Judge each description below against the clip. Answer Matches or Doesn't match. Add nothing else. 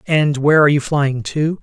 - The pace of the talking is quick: Matches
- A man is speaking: Matches